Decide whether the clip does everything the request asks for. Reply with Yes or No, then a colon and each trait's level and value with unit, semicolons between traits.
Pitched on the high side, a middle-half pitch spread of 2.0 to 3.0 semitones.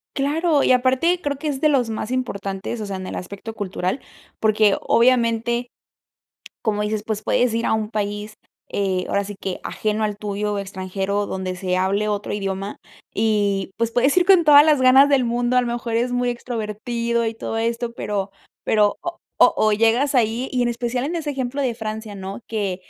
No: high, 225 Hz; average, 3.5 semitones